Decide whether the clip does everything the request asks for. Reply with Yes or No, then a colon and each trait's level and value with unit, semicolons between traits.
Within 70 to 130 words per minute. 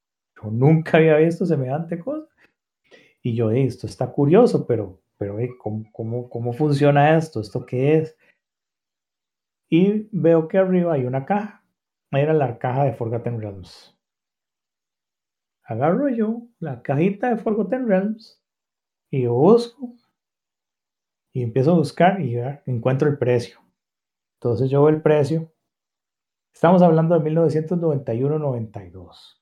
Yes: slow, 125 wpm